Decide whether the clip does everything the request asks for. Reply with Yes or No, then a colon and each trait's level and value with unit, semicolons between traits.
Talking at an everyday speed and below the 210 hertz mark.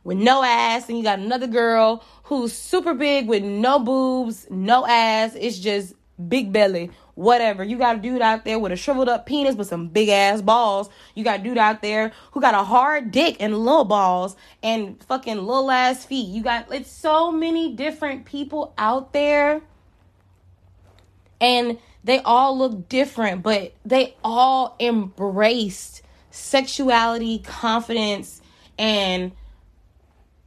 No: average, 150 wpm; high, 230 Hz